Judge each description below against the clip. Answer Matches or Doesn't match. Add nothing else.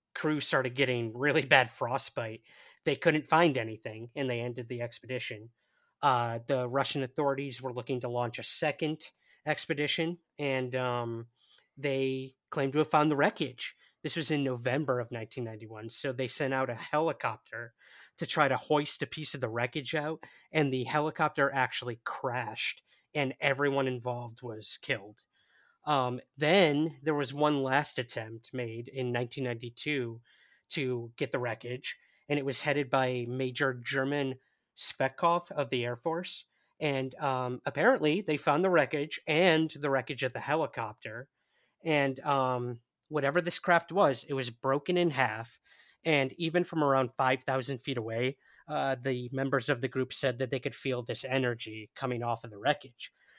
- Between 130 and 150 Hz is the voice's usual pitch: Matches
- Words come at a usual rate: Matches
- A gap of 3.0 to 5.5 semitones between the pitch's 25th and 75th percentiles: Matches